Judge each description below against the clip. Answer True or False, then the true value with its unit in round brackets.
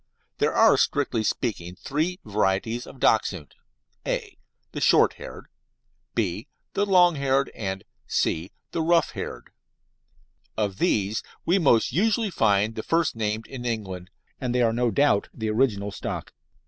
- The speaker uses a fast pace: False (145 wpm)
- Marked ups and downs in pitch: True (5.7 semitones)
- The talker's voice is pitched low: True (115 Hz)